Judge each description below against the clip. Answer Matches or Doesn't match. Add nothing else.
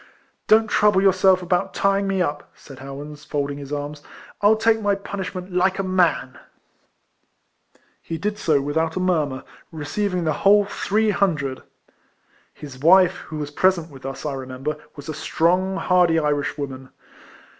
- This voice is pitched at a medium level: Matches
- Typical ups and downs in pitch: Matches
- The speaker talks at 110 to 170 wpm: Matches